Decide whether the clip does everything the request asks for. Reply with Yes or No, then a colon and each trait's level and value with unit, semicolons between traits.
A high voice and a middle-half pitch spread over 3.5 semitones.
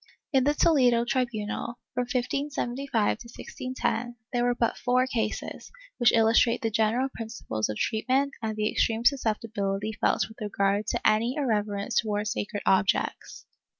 No: high, 230 Hz; average, 2.8 semitones